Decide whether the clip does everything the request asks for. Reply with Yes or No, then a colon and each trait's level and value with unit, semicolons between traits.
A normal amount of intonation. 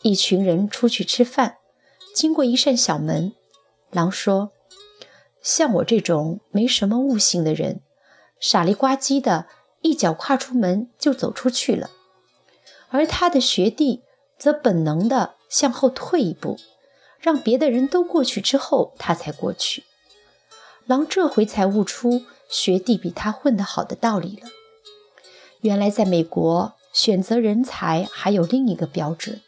No: wide, 6.1 semitones